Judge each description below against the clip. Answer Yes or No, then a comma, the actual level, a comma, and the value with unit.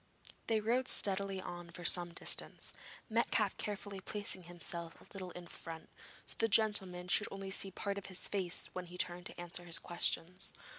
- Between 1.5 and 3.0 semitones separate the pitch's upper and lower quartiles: Yes, narrow, 2.4 semitones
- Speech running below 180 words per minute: No, average, 185 wpm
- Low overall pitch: No, medium, 185 Hz